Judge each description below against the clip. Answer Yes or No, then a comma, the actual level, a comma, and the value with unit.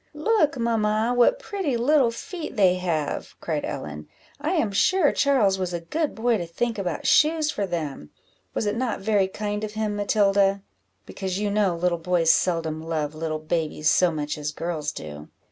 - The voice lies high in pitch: Yes, high, 195 Hz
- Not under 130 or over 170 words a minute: No, average, 180 wpm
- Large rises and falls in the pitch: Yes, wide, 5.9 semitones